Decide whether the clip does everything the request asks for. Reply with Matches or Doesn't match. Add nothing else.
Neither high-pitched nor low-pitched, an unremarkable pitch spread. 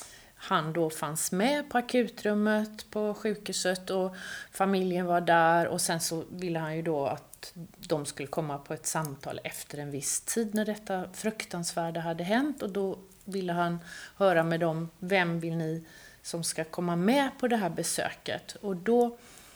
Matches